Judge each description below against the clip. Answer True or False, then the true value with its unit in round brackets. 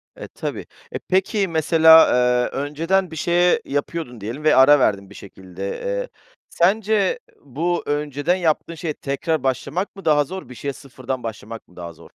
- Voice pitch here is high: False (150 Hz)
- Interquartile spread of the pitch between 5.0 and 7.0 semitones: True (5.6 semitones)